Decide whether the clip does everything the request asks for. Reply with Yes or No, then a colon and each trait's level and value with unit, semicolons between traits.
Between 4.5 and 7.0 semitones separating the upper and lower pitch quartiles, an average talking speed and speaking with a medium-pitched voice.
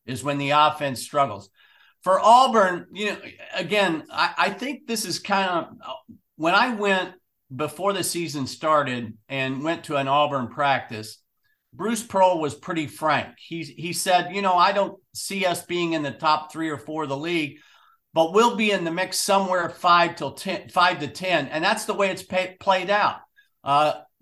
Yes: average, 5.0 semitones; average, 190 wpm; medium, 175 Hz